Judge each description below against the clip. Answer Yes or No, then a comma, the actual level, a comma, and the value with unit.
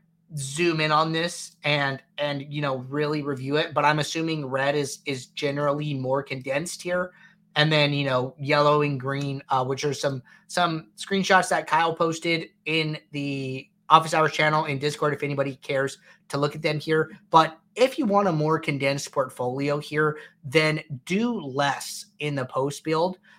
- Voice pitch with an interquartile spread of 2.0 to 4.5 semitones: Yes, average, 2.9 semitones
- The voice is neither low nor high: Yes, medium, 150 Hz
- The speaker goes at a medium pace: Yes, average, 175 wpm